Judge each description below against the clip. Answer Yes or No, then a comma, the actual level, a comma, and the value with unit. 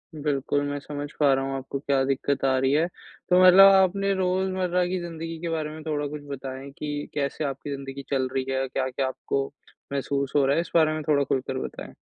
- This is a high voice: No, medium, 145 Hz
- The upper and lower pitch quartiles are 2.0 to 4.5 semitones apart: Yes, average, 3.4 semitones